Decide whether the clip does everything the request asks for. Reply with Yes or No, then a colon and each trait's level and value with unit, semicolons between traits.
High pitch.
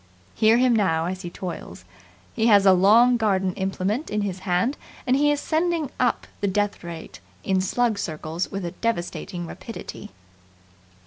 Yes: high, 200 Hz